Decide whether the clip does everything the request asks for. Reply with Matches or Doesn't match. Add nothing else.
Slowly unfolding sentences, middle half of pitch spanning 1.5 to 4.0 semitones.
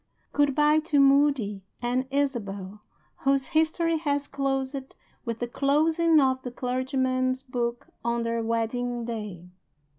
Matches